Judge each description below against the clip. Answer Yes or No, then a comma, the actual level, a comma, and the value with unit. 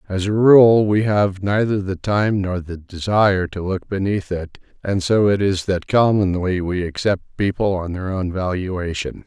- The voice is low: Yes, very low, 95 Hz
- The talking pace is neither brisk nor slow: Yes, average, 180 wpm